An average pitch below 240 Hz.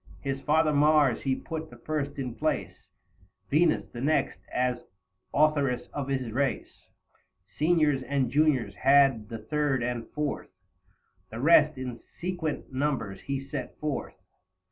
Yes: medium, 140 Hz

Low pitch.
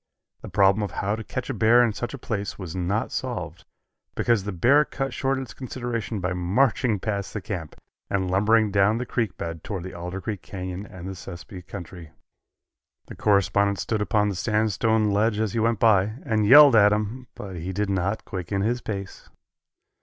Yes: low, 105 Hz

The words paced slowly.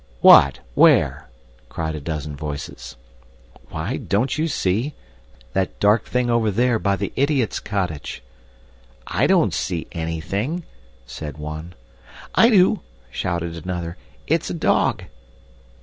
Yes: slow, 120 wpm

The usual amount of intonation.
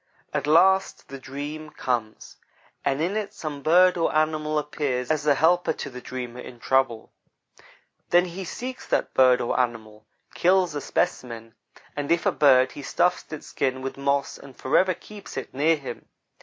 Yes: average, 4.6 semitones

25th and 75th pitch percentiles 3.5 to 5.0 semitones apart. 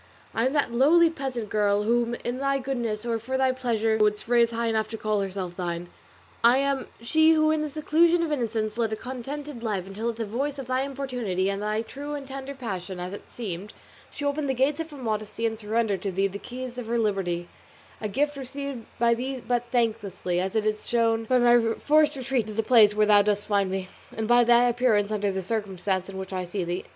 Yes: average, 4.2 semitones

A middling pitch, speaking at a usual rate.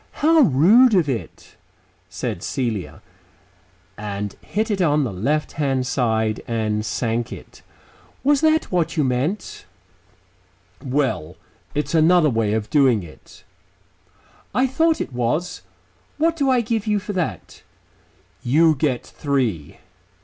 No: medium, 145 Hz; slow, 130 wpm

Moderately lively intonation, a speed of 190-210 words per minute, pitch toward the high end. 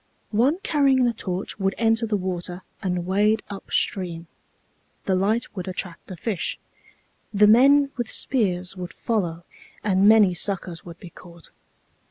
No: average, 3.8 semitones; average, 150 wpm; high, 195 Hz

